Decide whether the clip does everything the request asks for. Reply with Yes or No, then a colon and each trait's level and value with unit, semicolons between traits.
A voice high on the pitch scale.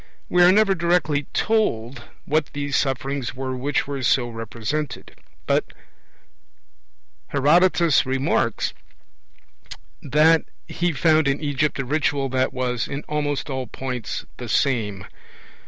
No: medium, 140 Hz